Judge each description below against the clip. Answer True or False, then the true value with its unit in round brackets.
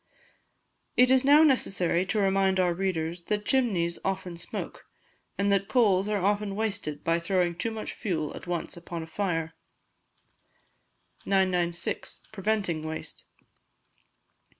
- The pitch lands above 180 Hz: True (190 Hz)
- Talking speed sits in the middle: False (125 wpm)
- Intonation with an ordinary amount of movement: True (3.2 semitones)